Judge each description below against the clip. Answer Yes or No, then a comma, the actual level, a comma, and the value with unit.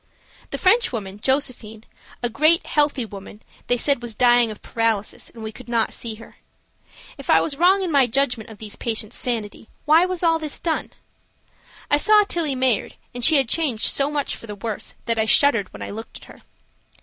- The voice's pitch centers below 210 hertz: No, high, 245 Hz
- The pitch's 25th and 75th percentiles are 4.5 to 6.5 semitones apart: Yes, average, 5.1 semitones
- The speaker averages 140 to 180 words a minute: No, average, 195 wpm